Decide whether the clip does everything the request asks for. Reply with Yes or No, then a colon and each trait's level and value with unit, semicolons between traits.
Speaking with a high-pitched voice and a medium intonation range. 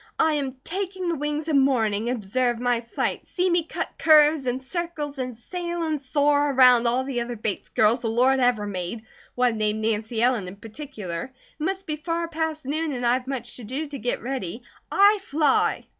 Yes: very high, 260 Hz; average, 4.7 semitones